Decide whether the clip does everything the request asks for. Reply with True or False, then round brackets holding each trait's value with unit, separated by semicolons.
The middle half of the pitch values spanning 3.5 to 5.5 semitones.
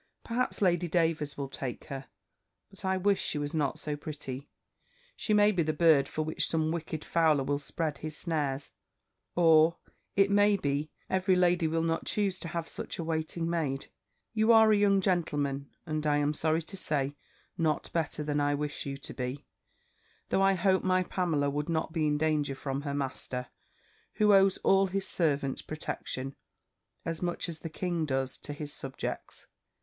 True (3.8 semitones)